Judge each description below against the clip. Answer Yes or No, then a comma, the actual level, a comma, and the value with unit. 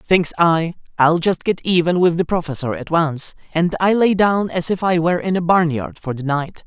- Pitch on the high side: No, medium, 170 Hz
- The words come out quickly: Yes, fast, 225 wpm